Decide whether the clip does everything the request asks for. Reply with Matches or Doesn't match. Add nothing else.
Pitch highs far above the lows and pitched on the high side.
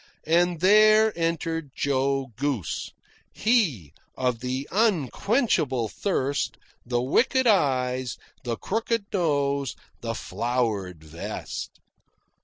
Doesn't match